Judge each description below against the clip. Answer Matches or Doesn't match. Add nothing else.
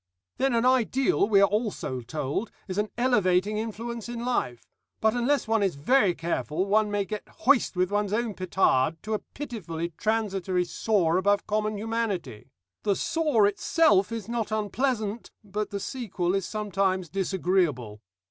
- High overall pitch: Matches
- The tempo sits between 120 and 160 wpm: Matches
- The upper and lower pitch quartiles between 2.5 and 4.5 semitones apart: Matches